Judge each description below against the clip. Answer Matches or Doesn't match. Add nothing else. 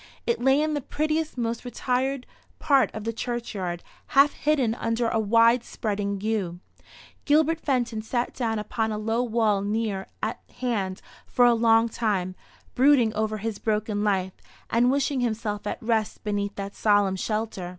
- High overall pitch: Matches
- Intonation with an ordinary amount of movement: Matches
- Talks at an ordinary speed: Matches